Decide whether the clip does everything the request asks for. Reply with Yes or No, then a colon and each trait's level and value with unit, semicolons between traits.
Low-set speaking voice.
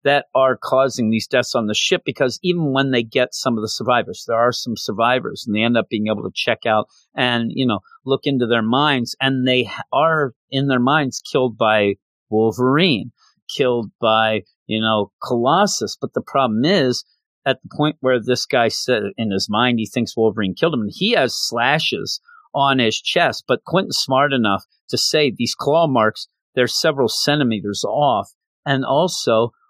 Yes: low, 125 Hz